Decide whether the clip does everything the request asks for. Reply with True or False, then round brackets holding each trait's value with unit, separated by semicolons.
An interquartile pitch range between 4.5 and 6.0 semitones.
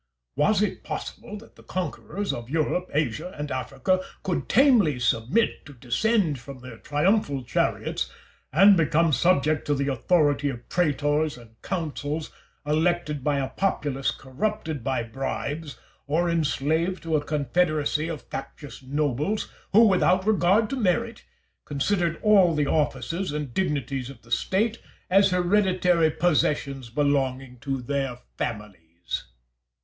True (5.0 semitones)